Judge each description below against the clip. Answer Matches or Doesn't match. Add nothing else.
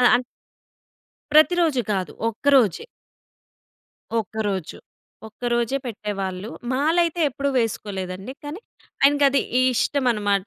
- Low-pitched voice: Doesn't match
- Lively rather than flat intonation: Matches